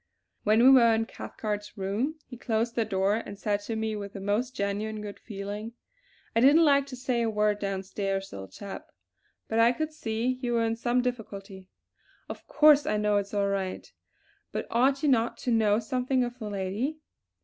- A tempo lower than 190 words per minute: No, average, 195 wpm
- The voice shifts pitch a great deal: No, average, 3.4 semitones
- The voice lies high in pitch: Yes, high, 220 Hz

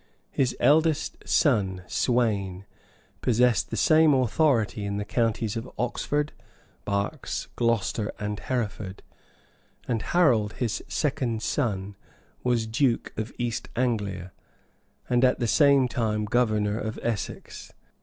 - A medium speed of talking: No, slow, 115 wpm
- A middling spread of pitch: Yes, average, 3.5 semitones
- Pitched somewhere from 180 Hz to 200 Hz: No, low, 115 Hz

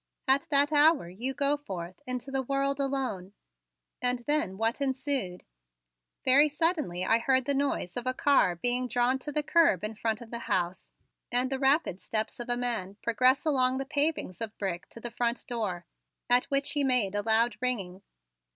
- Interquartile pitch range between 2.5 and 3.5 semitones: No, average, 4.2 semitones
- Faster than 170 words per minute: Yes, average, 185 wpm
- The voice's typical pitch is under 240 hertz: No, very high, 250 Hz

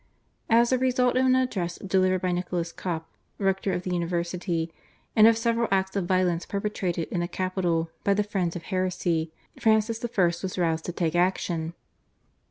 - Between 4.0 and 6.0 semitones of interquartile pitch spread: No, average, 3.3 semitones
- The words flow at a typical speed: Yes, average, 175 wpm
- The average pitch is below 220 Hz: Yes, medium, 185 Hz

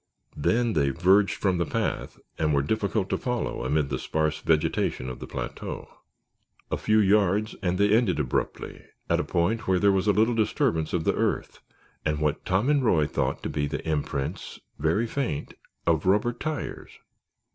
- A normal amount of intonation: No, wide, 5.9 semitones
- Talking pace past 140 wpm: Yes, average, 180 wpm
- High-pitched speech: No, very low, 95 Hz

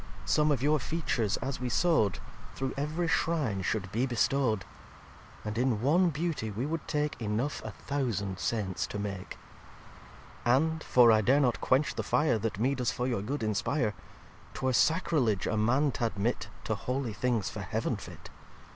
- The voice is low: Yes, low, 125 Hz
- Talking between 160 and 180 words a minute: Yes, average, 170 wpm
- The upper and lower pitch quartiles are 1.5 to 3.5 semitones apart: No, average, 5.2 semitones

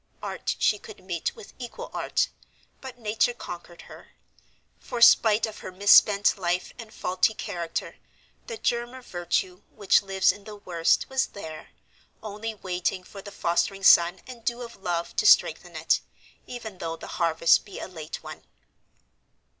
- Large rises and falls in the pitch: No, average, 4.2 semitones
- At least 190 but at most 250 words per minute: No, average, 160 wpm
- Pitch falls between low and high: No, high, 200 Hz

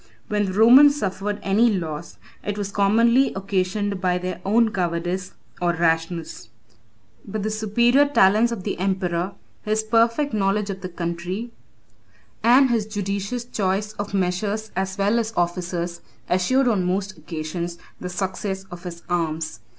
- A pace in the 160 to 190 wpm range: No, average, 145 wpm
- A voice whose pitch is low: No, high, 195 Hz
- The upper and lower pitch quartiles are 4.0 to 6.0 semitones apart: No, average, 3.3 semitones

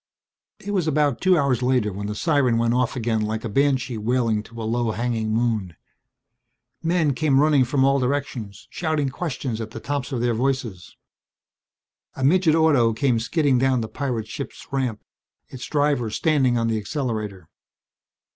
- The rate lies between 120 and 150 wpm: No, average, 165 wpm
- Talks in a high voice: No, low, 125 Hz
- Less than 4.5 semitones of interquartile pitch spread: Yes, average, 4.1 semitones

